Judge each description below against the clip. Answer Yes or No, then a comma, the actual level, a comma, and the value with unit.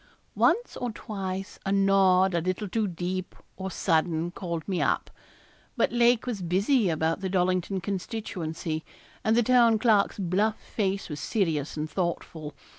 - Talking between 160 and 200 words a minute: No, average, 150 wpm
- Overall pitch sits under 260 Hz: Yes, high, 190 Hz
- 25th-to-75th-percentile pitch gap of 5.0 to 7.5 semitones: No, average, 3.5 semitones